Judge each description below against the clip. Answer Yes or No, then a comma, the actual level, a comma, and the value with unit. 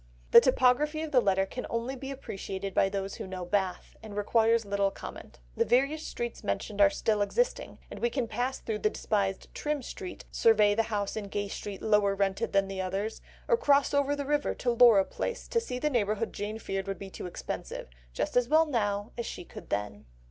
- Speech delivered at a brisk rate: Yes, fast, 210 wpm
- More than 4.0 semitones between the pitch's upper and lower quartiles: Yes, average, 4.5 semitones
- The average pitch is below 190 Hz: No, high, 215 Hz